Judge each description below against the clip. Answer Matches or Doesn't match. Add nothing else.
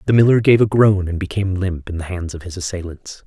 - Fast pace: Matches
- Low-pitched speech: Matches